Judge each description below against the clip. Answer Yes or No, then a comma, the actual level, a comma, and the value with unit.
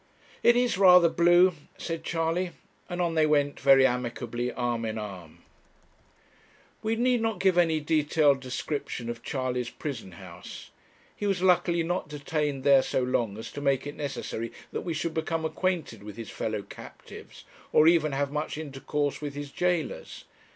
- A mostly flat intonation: No, average, 5.3 semitones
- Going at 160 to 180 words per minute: Yes, average, 165 wpm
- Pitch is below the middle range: No, medium, 150 Hz